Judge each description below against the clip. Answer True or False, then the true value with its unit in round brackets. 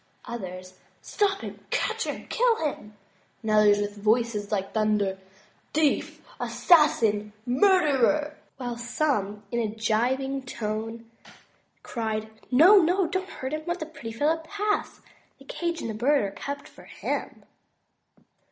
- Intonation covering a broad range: True (6.4 semitones)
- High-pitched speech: True (240 Hz)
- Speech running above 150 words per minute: False (145 wpm)